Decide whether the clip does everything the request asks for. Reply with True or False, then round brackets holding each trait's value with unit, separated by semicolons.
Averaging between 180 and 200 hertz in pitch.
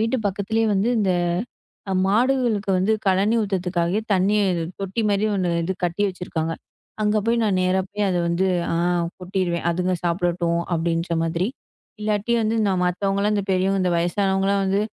True (190 Hz)